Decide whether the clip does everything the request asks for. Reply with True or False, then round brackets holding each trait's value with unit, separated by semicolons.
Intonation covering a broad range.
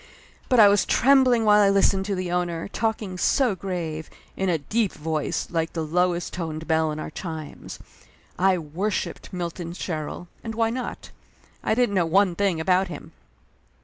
False (3.8 semitones)